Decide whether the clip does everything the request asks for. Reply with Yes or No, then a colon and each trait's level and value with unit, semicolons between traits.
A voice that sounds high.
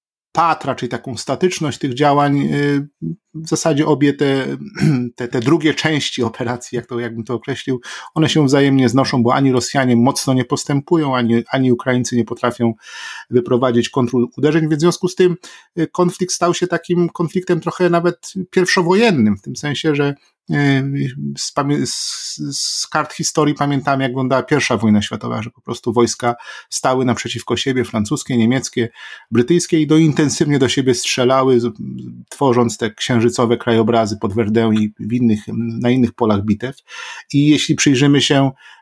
No: low, 135 Hz